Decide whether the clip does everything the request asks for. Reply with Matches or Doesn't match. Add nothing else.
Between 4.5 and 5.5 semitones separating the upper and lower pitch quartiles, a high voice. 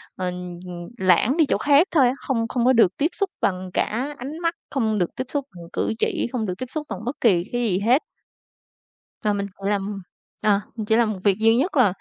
Matches